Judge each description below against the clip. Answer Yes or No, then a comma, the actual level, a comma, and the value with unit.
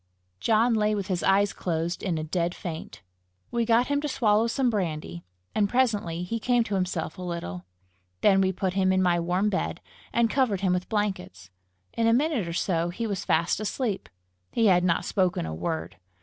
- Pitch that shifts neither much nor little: Yes, average, 4.4 semitones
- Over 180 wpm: Yes, average, 195 wpm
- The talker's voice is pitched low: No, high, 190 Hz